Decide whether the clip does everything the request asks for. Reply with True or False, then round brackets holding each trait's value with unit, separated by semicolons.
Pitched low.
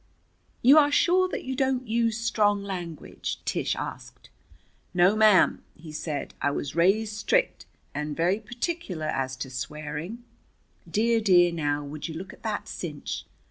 False (190 Hz)